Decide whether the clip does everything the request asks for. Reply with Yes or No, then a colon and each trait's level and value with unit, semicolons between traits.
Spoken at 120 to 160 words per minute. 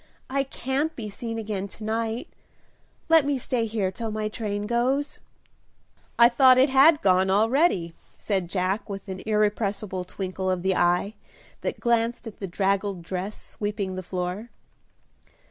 Yes: average, 150 wpm